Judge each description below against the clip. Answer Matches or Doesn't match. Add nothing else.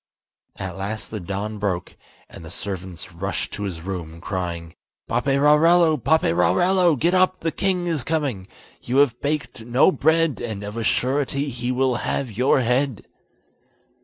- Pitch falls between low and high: Doesn't match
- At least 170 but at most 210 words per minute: Doesn't match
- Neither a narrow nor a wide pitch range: Doesn't match